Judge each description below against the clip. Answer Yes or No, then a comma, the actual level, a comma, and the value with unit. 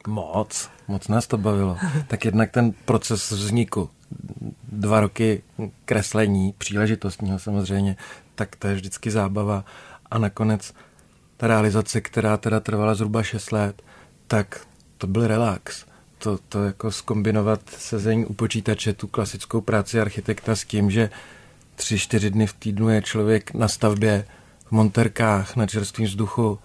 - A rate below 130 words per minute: No, average, 140 wpm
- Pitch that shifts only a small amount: Yes, narrow, 1.4 semitones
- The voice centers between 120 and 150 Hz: No, low, 110 Hz